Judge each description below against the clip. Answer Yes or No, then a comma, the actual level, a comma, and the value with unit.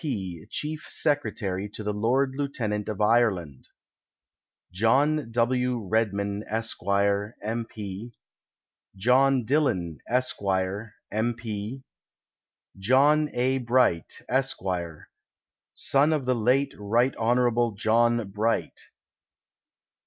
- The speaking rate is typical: No, slow, 95 wpm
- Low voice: Yes, low, 115 Hz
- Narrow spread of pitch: No, average, 3.9 semitones